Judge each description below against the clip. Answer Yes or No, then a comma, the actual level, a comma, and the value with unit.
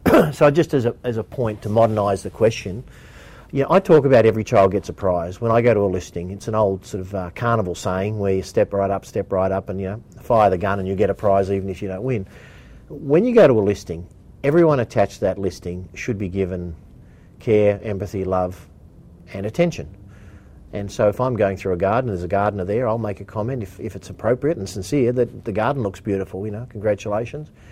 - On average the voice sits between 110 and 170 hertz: No, low, 100 Hz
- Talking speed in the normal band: No, fast, 235 wpm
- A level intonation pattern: No, average, 3.1 semitones